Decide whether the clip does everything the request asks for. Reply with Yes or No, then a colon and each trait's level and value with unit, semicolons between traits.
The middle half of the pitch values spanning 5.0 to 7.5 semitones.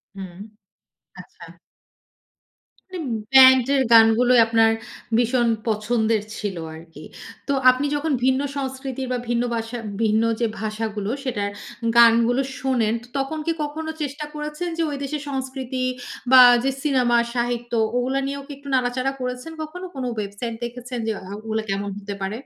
No: average, 3.2 semitones